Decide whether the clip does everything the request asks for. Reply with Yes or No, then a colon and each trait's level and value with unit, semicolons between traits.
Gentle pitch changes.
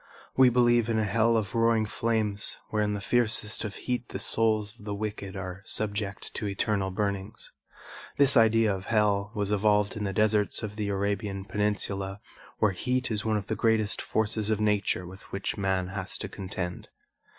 Yes: narrow, 1.9 semitones